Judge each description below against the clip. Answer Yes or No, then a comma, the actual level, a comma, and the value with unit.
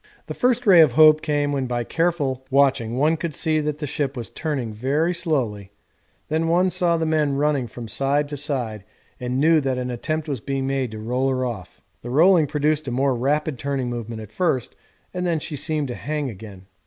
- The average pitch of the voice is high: No, medium, 140 Hz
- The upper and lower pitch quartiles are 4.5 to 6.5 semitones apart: No, average, 3.9 semitones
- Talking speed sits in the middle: No, fast, 210 wpm